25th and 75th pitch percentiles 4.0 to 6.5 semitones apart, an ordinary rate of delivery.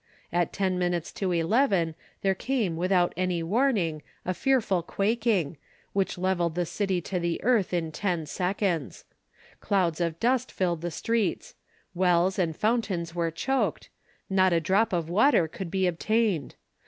No: average, 3.1 semitones; average, 150 wpm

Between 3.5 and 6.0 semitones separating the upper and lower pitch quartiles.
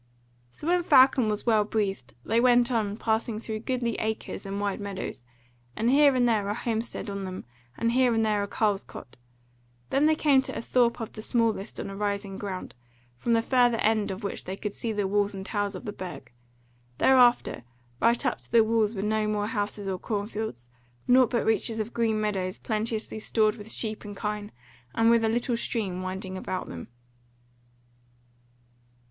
No: narrow, 2.5 semitones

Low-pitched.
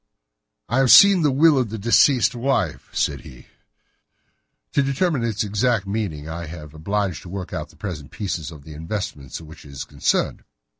Yes: low, 100 Hz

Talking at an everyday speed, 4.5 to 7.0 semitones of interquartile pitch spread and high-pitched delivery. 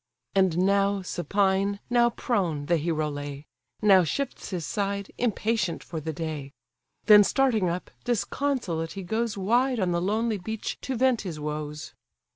Yes: average, 150 wpm; average, 5.3 semitones; high, 195 Hz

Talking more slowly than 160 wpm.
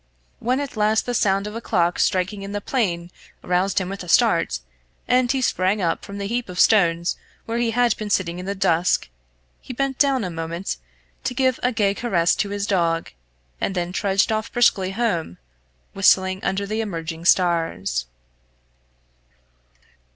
No: average, 175 wpm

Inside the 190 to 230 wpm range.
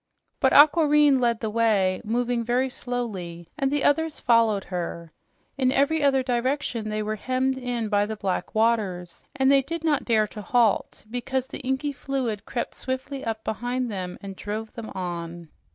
No: average, 170 wpm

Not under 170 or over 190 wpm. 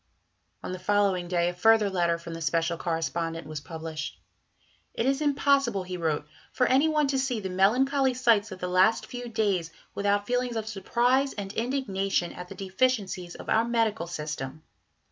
Yes: average, 175 wpm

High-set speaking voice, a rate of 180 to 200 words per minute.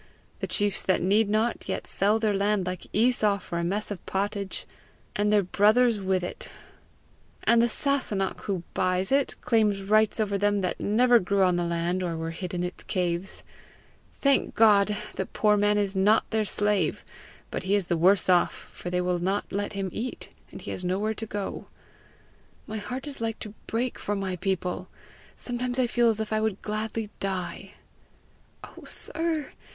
Yes: high, 205 Hz; average, 185 wpm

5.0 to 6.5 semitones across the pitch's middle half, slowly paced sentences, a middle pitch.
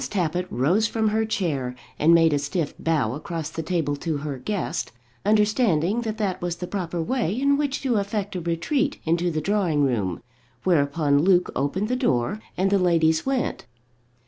No: wide, 5.4 semitones; average, 175 wpm; medium, 175 Hz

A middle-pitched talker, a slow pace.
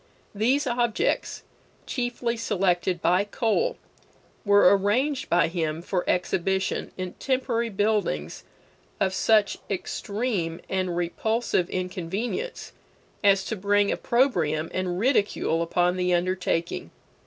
No: high, 195 Hz; slow, 105 wpm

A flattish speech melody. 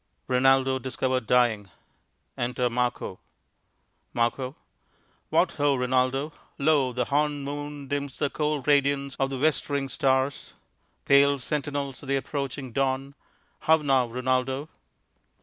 Yes: narrow, 1.9 semitones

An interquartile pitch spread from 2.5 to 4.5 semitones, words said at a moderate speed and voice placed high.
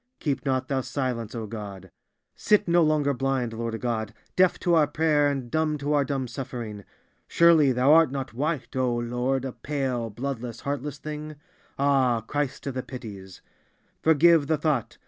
No: average, 3.8 semitones; average, 165 wpm; low, 135 Hz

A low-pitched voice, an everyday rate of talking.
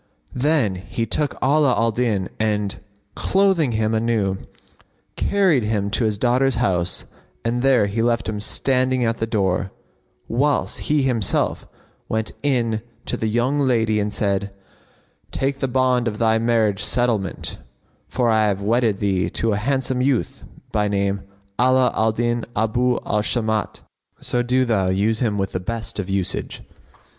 Yes: low, 115 Hz; average, 155 wpm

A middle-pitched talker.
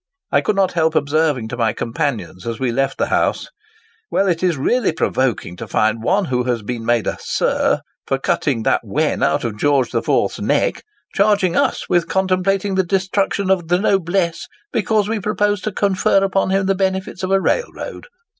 Yes: medium, 175 Hz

